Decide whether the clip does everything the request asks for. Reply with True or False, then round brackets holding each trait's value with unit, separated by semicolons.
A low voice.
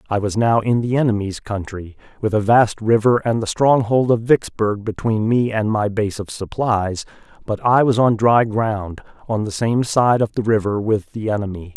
True (110 Hz)